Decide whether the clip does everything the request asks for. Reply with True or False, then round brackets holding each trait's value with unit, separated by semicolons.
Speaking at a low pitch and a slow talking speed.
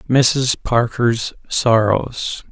True (120 Hz; 70 wpm)